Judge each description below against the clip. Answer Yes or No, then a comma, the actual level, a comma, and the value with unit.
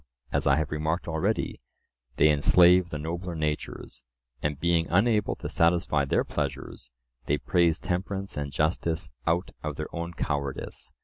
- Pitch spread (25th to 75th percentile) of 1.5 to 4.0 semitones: Yes, average, 2.9 semitones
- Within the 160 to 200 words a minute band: No, average, 145 wpm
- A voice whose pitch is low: Yes, very low, 80 Hz